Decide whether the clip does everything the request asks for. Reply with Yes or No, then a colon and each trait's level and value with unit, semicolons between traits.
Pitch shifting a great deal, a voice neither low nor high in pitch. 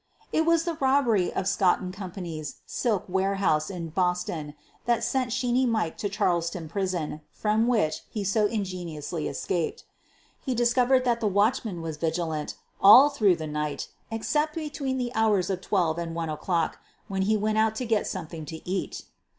No: wide, 5.7 semitones; high, 195 Hz